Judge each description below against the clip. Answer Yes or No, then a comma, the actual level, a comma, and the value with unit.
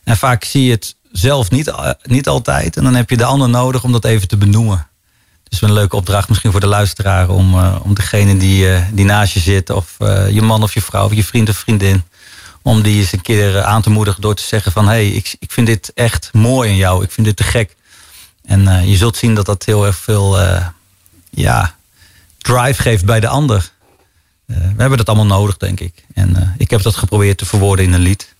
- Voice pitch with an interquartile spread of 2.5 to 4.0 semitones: Yes, average, 2.8 semitones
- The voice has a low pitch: Yes, low, 105 Hz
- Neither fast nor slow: No, fast, 240 wpm